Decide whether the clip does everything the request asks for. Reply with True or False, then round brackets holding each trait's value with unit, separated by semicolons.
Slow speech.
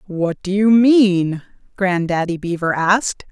True (125 wpm)